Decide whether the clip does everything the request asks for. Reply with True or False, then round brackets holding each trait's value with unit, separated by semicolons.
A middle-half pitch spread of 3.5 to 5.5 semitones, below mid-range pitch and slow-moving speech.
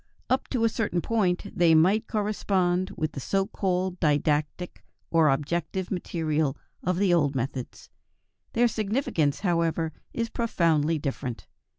False (4.2 semitones; 175 Hz; 130 wpm)